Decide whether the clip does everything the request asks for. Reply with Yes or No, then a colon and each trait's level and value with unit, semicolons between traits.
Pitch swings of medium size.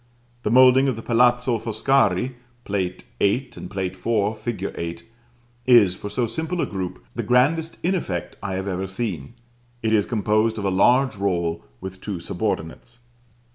Yes: average, 4.6 semitones